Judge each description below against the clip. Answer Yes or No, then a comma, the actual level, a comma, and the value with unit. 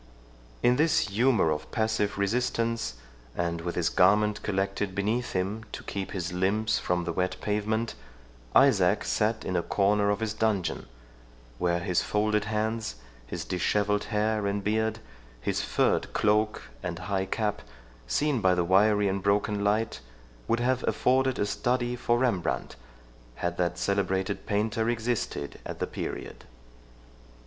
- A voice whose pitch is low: Yes, low, 105 Hz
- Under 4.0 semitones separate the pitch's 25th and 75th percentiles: Yes, average, 2.7 semitones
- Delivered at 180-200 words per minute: No, average, 145 wpm